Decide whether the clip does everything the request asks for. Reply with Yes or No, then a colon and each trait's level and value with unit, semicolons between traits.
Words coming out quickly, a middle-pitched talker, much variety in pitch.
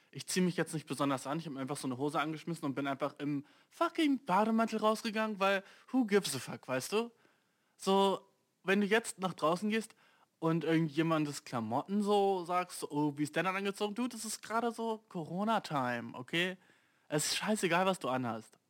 Yes: fast, 195 wpm; medium, 180 Hz; wide, 6.3 semitones